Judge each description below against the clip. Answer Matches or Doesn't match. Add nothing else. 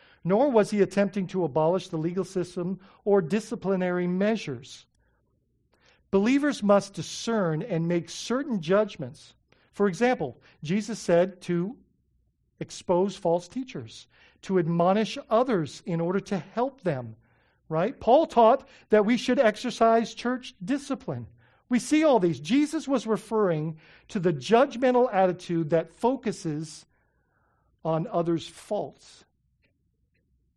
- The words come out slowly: Matches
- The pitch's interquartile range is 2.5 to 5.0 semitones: Doesn't match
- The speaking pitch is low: Doesn't match